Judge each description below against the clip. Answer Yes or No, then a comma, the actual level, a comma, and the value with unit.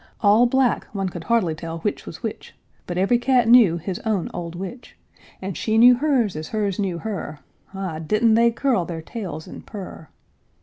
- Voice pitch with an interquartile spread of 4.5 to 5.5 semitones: Yes, average, 5.2 semitones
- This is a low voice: No, high, 200 Hz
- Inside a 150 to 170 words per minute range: No, average, 185 wpm